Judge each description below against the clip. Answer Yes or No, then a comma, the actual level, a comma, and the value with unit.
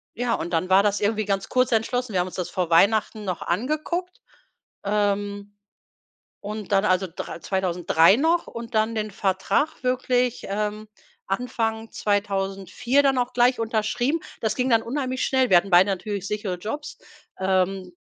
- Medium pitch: No, high, 210 Hz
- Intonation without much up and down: No, average, 4.2 semitones